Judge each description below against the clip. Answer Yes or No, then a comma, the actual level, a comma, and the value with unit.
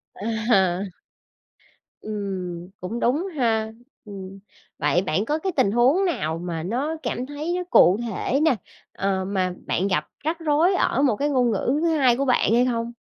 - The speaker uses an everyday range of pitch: No, wide, 7.1 semitones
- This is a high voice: Yes, high, 230 Hz